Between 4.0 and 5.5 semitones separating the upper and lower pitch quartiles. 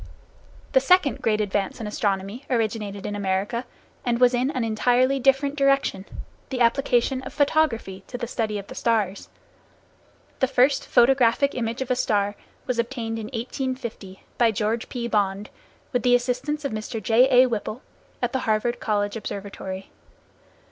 No: average, 3.5 semitones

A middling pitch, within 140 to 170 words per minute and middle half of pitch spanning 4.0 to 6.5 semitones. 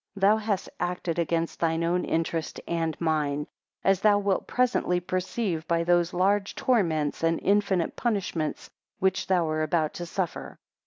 No: medium, 175 Hz; average, 155 wpm; average, 3.0 semitones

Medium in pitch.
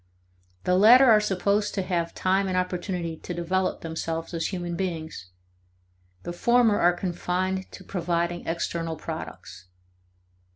Yes: medium, 180 Hz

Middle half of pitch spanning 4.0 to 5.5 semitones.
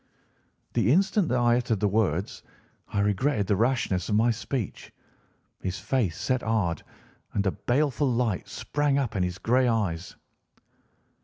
Yes: average, 4.6 semitones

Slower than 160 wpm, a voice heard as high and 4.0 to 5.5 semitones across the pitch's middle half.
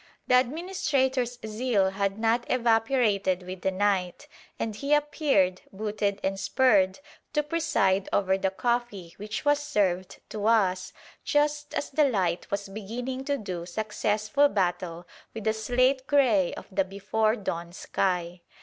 Yes: average, 140 wpm; high, 215 Hz; average, 5.0 semitones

